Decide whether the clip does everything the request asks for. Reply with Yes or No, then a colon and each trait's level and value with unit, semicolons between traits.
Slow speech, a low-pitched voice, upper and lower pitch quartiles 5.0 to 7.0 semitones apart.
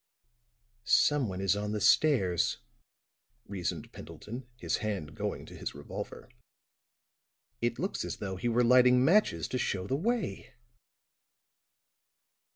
Yes: slow, 120 wpm; low, 115 Hz; average, 5.3 semitones